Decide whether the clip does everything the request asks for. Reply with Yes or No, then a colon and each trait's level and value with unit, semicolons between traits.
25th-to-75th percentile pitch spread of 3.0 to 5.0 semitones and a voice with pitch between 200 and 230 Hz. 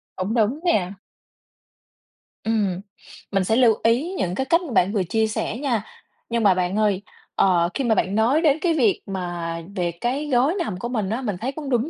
No: wide, 5.5 semitones; high, 220 Hz